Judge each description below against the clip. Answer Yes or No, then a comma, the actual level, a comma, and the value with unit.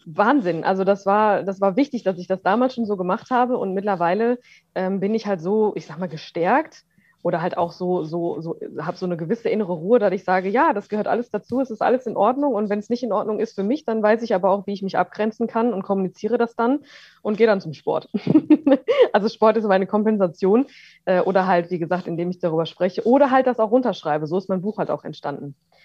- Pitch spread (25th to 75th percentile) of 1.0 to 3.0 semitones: No, average, 4.3 semitones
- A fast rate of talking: Yes, fast, 245 wpm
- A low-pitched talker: No, high, 200 Hz